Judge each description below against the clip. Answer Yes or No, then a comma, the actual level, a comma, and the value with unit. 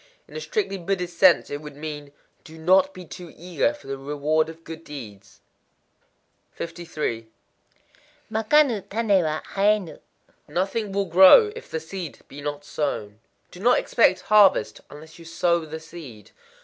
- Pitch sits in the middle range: Yes, medium, 170 Hz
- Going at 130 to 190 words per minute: Yes, average, 150 wpm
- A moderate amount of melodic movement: Yes, average, 4.7 semitones